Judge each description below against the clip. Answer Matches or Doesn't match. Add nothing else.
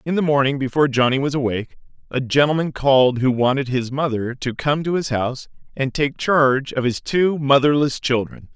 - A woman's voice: Doesn't match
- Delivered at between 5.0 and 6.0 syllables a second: Matches